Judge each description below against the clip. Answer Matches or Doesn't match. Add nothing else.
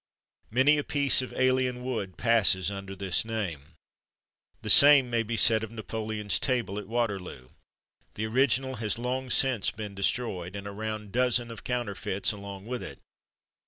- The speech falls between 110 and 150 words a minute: Doesn't match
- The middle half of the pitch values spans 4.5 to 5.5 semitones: Doesn't match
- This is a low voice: Matches